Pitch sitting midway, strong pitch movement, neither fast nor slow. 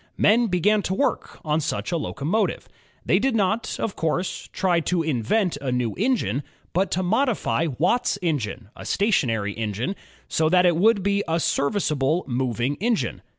Yes: medium, 170 Hz; wide, 6.5 semitones; average, 160 wpm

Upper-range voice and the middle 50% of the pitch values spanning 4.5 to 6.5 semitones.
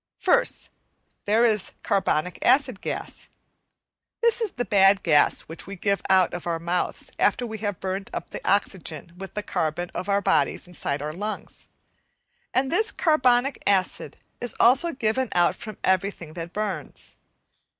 Yes: high, 200 Hz; average, 5.1 semitones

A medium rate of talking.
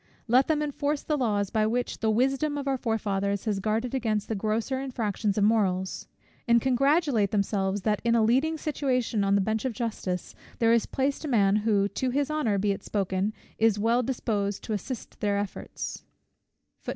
Yes: average, 185 wpm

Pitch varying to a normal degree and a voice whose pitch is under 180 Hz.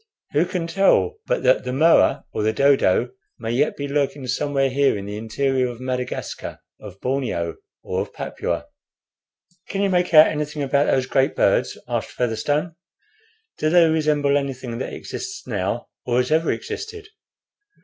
Yes: average, 3.7 semitones; medium, 140 Hz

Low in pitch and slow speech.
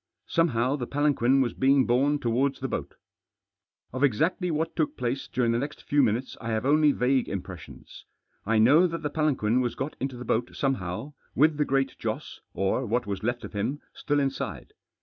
No: low, 130 Hz; average, 190 wpm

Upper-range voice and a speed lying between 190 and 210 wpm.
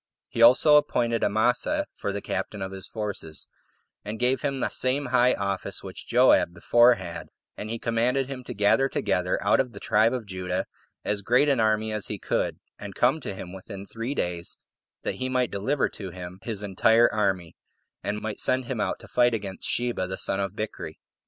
No: low, 110 Hz; average, 195 wpm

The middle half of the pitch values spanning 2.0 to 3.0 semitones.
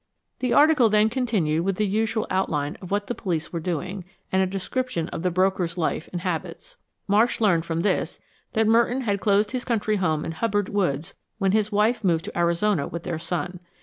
No: average, 4.2 semitones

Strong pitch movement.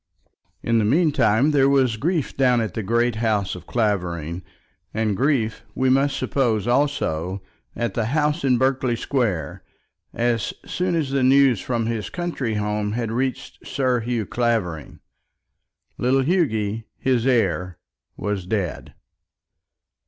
No: average, 4.1 semitones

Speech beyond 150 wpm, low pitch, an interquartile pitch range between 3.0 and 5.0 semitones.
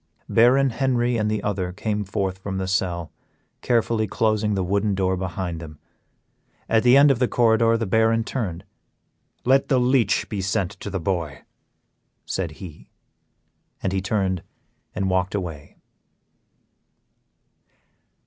No: average, 140 wpm; low, 100 Hz; average, 3.6 semitones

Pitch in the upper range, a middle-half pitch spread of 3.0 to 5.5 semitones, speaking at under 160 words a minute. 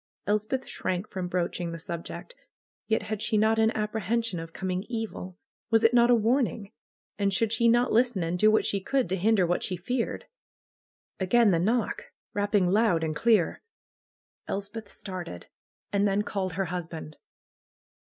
No: high, 205 Hz; average, 3.8 semitones; average, 165 wpm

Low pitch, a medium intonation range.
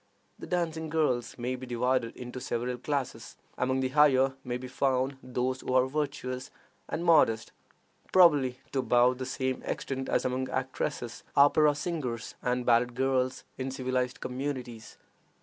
No: low, 130 Hz; narrow, 1.7 semitones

